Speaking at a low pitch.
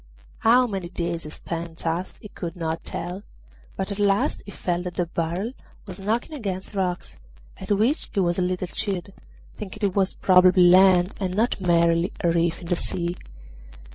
No: medium, 185 Hz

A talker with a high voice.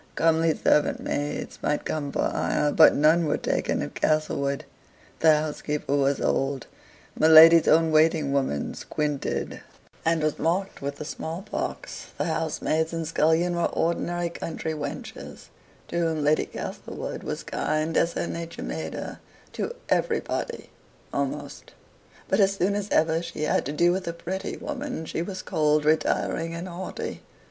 No: medium, 160 Hz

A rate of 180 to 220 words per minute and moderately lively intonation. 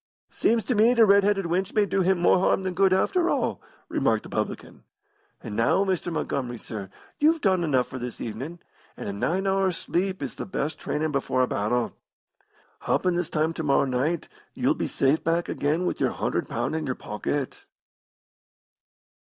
No: average, 185 wpm; wide, 6.1 semitones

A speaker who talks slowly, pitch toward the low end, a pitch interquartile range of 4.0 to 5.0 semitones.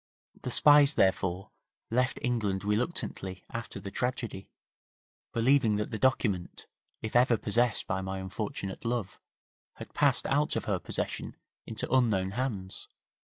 Yes: slow, 130 wpm; low, 110 Hz; average, 4.4 semitones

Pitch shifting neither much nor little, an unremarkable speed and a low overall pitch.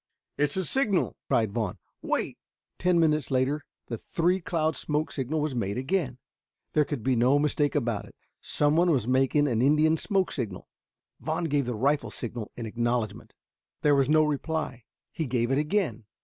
No: average, 4.3 semitones; average, 170 wpm; medium, 145 Hz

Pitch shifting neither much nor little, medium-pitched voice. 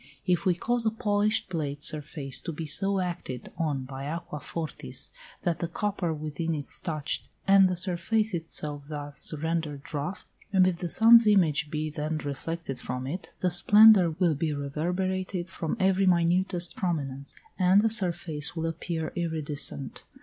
Yes: average, 3.8 semitones; medium, 165 Hz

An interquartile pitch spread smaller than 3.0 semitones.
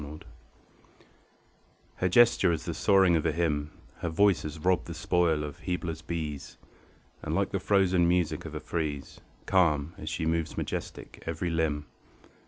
Yes: narrow, 2.4 semitones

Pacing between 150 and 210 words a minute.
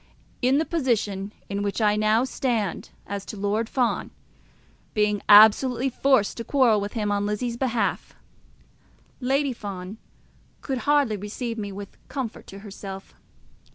No: average, 140 wpm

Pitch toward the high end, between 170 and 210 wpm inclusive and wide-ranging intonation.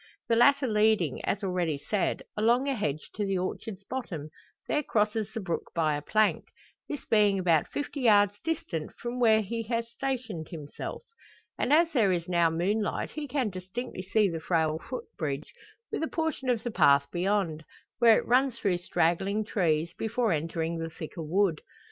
Yes: high, 205 Hz; average, 175 wpm; wide, 5.8 semitones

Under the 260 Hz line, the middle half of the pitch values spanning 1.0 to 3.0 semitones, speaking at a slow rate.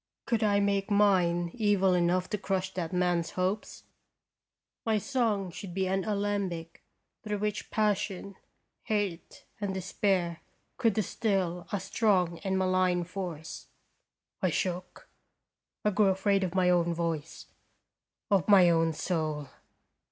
Yes: high, 190 Hz; narrow, 2.6 semitones; slow, 130 wpm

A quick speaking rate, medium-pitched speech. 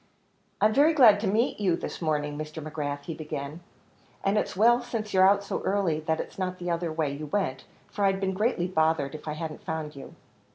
Yes: fast, 215 wpm; medium, 170 Hz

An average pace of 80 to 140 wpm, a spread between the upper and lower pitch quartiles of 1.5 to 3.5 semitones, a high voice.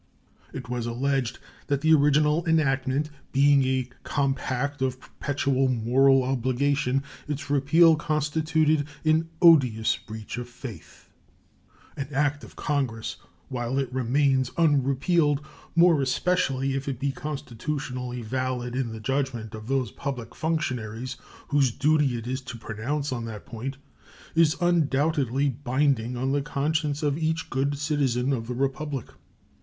No: slow, 135 wpm; average, 2.7 semitones; low, 135 Hz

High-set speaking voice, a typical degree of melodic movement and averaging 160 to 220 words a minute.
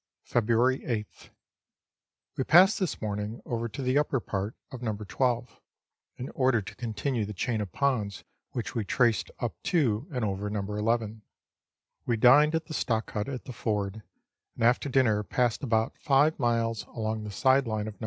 No: low, 115 Hz; average, 3.5 semitones; average, 175 wpm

